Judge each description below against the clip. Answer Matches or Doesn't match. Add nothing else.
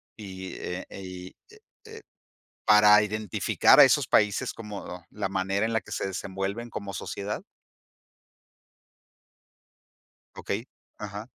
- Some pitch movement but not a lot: Doesn't match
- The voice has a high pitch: Doesn't match